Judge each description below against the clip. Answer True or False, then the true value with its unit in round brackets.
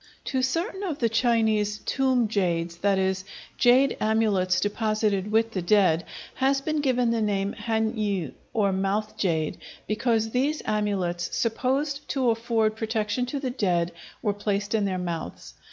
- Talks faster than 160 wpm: False (145 wpm)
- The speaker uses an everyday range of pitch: True (3.9 semitones)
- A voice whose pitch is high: True (215 Hz)